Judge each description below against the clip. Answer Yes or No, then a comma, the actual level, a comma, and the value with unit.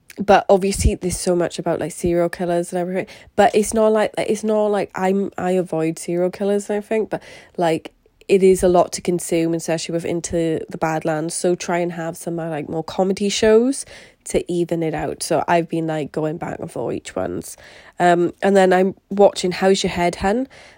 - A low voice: No, medium, 180 Hz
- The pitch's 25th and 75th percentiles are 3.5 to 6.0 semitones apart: No, average, 2.9 semitones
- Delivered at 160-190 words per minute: No, fast, 205 wpm